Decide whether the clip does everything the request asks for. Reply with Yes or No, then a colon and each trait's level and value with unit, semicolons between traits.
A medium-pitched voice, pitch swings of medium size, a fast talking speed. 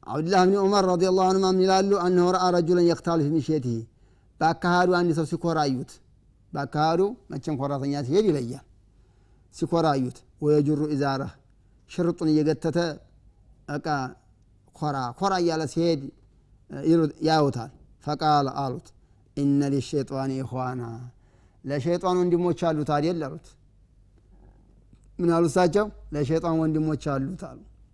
Yes: medium, 150 Hz; average, 4.8 semitones; fast, 140 wpm